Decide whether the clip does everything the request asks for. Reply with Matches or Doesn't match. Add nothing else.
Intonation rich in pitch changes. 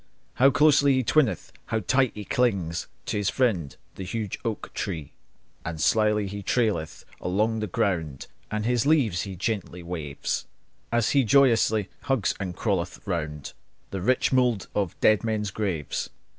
Doesn't match